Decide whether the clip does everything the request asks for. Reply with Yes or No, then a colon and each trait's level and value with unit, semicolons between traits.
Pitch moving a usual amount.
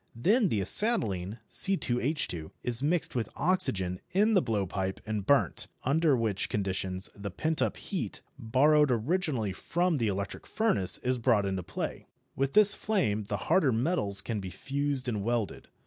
No: wide, 7.9 semitones